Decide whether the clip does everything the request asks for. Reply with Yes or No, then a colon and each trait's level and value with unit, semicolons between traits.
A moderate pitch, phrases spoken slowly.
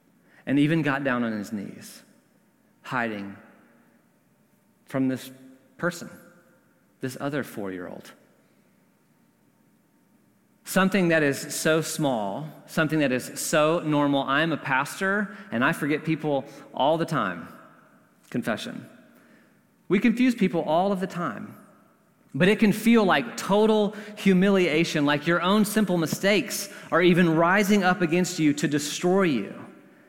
Yes: medium, 175 Hz; slow, 130 wpm